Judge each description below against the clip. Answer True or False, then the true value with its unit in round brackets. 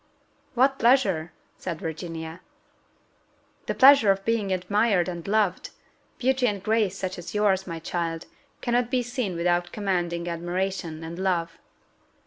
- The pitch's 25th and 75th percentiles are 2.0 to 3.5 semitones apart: False (4.2 semitones)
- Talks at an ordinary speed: False (130 wpm)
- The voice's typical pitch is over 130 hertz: True (190 Hz)